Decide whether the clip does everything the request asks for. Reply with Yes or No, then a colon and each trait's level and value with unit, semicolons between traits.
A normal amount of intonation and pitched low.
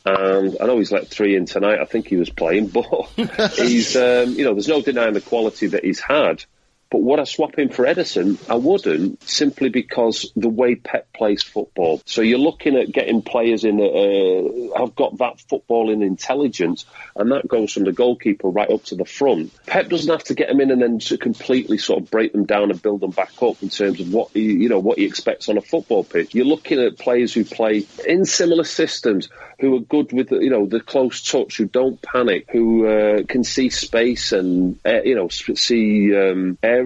Yes: average, 4.4 semitones; low, 120 Hz